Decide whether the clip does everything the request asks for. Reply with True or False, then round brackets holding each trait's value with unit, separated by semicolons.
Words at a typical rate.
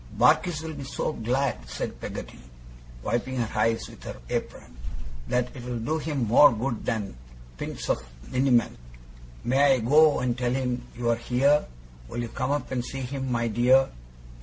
True (170 wpm)